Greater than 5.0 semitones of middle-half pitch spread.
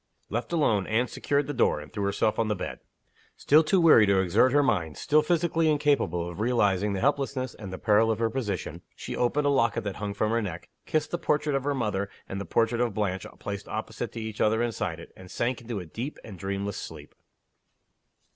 Yes: wide, 5.5 semitones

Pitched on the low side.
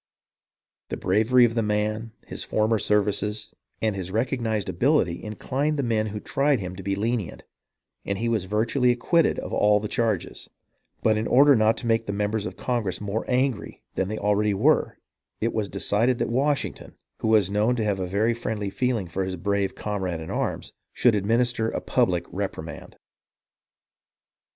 Yes: low, 110 Hz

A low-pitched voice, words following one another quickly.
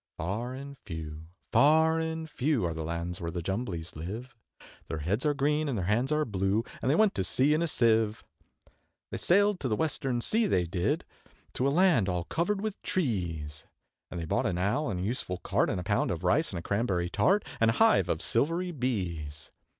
Yes: low, 115 Hz; fast, 210 wpm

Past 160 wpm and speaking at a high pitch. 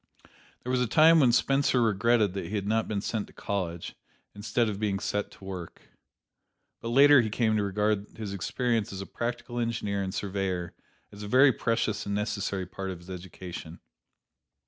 No: average, 185 wpm; low, 105 Hz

